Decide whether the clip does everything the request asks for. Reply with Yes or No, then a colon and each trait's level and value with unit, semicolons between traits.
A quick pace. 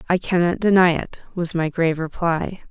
No: average, 180 wpm